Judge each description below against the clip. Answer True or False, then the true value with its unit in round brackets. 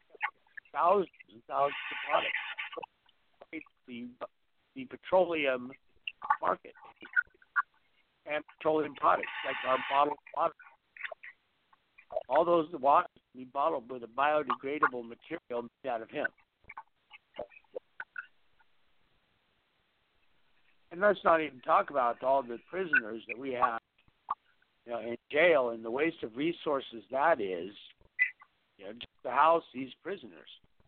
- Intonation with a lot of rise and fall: True (5.9 semitones)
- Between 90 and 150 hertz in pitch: True (140 Hz)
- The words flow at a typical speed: False (115 wpm)